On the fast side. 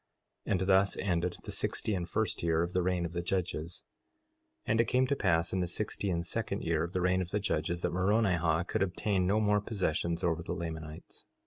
Yes: fast, 225 wpm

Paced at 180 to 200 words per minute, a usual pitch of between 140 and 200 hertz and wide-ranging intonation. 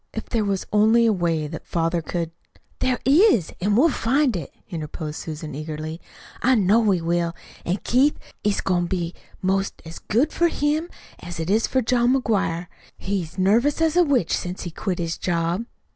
Yes: average, 190 wpm; high, 190 Hz; wide, 6.1 semitones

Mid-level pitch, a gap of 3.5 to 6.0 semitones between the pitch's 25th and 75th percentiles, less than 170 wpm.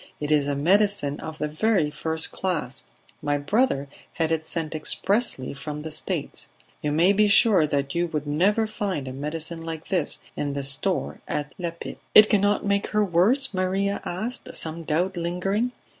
No: medium, 165 Hz; average, 5.1 semitones; average, 175 wpm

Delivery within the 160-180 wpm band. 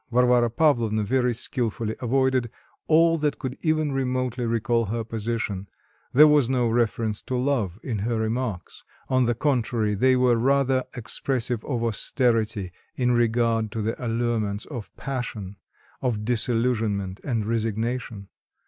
No: slow, 135 wpm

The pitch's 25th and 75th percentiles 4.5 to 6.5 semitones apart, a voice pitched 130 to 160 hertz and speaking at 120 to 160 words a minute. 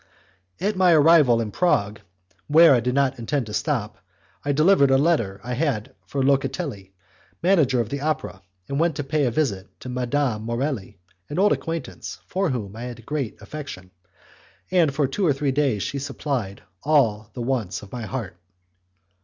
No: average, 4.8 semitones; low, 135 Hz; average, 175 wpm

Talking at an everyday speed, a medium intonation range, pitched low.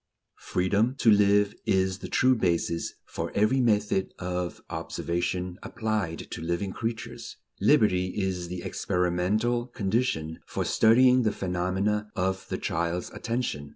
No: slow, 125 wpm; average, 3.6 semitones; very low, 95 Hz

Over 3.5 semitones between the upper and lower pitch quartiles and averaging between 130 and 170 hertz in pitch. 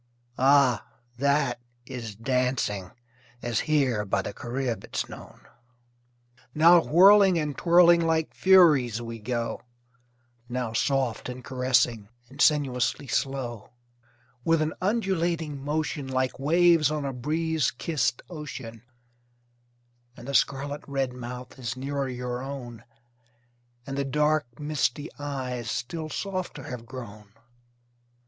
Yes: average, 4.0 semitones; low, 135 Hz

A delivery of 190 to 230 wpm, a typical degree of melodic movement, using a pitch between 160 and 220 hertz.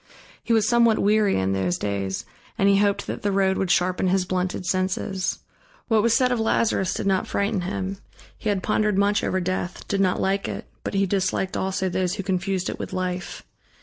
No: fast, 205 wpm; narrow, 1.7 semitones; high, 190 Hz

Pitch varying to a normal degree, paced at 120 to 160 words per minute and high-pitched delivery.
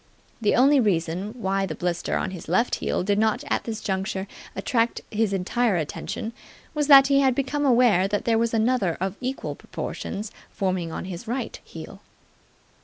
No: average, 4.5 semitones; average, 175 wpm; high, 210 Hz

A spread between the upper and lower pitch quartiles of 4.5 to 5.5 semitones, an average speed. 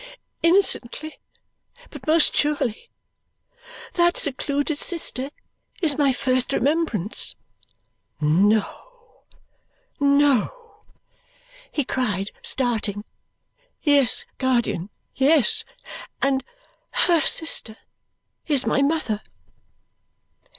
No: average, 4.9 semitones; slow, 75 wpm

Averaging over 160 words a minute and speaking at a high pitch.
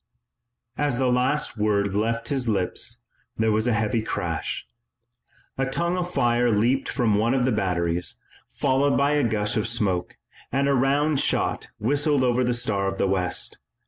No: average, 170 wpm; low, 120 Hz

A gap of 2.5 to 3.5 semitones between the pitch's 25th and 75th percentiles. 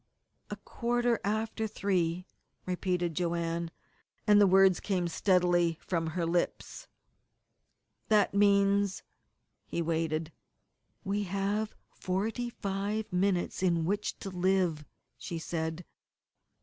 Yes: average, 3.0 semitones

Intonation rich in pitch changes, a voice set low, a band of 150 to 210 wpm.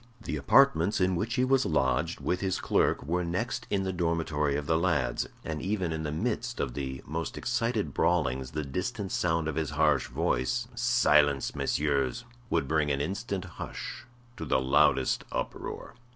Yes: wide, 5.7 semitones; very low, 80 Hz; average, 170 wpm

